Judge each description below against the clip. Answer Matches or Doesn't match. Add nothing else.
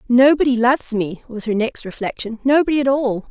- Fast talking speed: Doesn't match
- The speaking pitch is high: Matches